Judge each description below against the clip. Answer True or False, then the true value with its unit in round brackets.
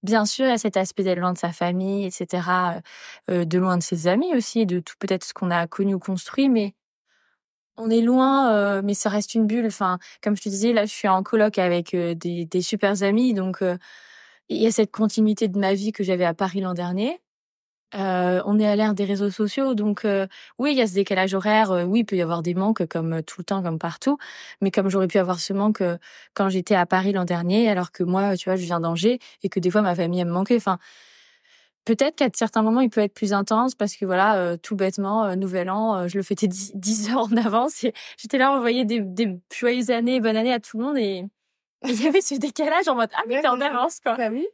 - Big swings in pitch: False (3.7 semitones)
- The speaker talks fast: True (255 wpm)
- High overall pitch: True (205 Hz)